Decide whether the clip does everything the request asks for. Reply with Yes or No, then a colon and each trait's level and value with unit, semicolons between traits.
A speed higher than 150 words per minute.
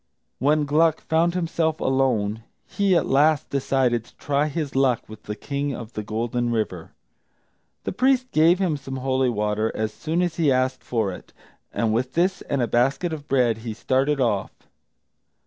Yes: average, 175 wpm